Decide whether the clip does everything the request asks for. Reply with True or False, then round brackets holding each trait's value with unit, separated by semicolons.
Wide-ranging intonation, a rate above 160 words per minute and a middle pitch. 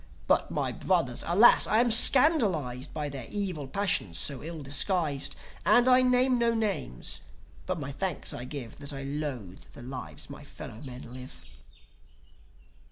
False (8.1 semitones; 155 wpm; 150 Hz)